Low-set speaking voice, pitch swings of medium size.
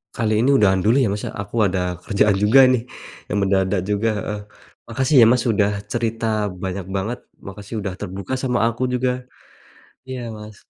Yes: low, 105 Hz; average, 3.4 semitones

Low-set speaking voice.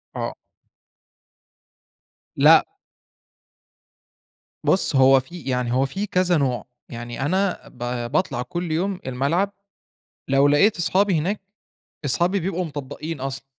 No: medium, 155 Hz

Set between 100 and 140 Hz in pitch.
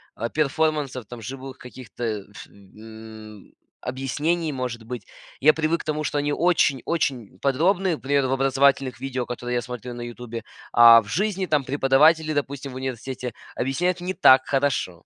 Yes: low, 135 Hz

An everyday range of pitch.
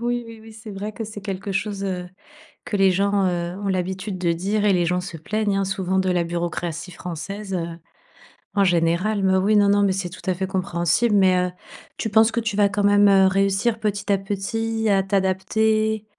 No: narrow, 2.2 semitones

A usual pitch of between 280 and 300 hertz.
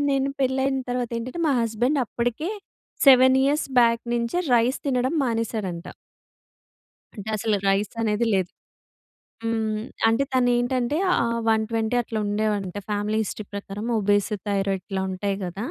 No: high, 225 Hz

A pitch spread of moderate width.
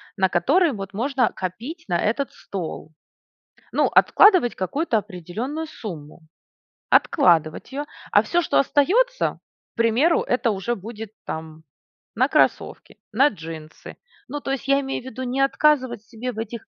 No: wide, 6.6 semitones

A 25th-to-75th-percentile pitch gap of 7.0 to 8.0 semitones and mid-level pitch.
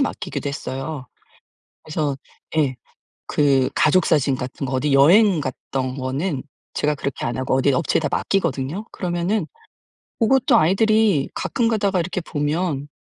No: wide, 5.4 semitones; medium, 150 Hz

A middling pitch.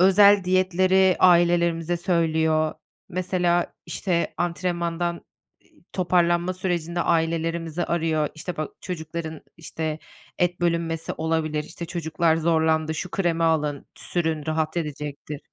Yes: medium, 170 Hz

